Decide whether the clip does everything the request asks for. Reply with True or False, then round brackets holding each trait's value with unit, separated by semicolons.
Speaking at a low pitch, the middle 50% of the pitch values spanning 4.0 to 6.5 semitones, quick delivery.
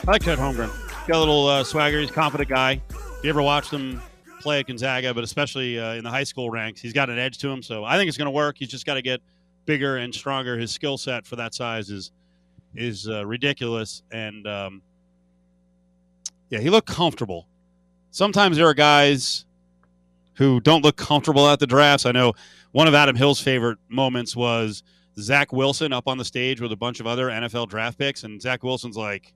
True (125 Hz; 4.6 semitones; 215 wpm)